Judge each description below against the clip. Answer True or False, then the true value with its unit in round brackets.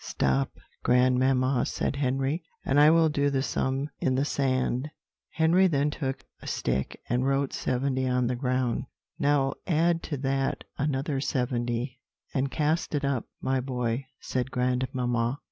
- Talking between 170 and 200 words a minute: False (145 wpm)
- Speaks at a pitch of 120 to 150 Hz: True (135 Hz)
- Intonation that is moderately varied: False (2.1 semitones)